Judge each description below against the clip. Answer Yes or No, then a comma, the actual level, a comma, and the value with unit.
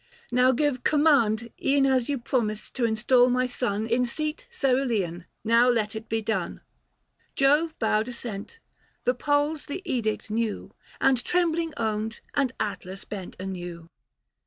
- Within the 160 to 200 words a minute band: No, average, 140 wpm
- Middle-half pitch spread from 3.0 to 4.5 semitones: Yes, average, 4.2 semitones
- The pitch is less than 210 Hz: No, high, 240 Hz